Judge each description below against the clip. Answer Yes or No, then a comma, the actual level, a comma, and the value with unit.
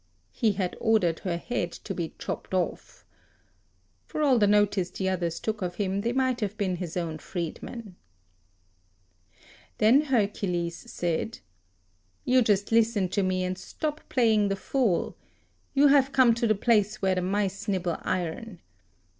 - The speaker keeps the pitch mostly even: No, average, 4.1 semitones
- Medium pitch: No, high, 200 Hz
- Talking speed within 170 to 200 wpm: No, average, 155 wpm